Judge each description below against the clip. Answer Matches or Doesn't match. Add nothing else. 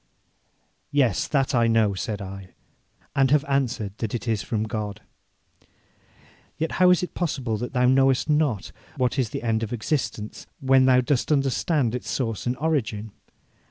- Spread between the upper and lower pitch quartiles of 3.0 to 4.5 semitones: Matches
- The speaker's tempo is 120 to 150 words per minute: Doesn't match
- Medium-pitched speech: Doesn't match